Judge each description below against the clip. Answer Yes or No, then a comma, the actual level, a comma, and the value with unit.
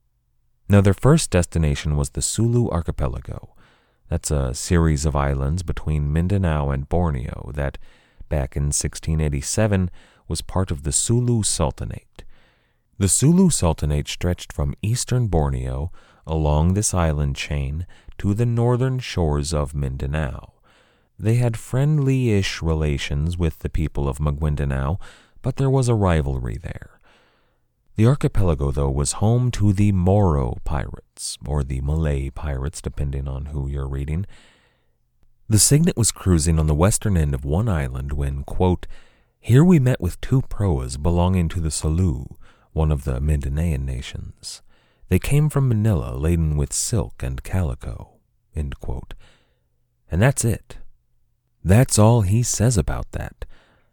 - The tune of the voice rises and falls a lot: Yes, wide, 6.8 semitones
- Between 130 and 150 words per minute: Yes, average, 140 wpm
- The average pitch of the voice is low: Yes, very low, 85 Hz